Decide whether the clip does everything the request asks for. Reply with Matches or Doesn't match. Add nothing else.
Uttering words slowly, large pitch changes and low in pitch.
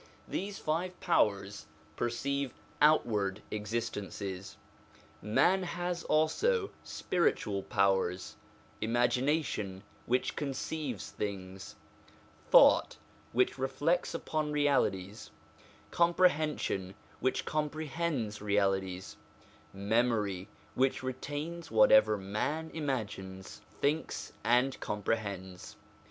Matches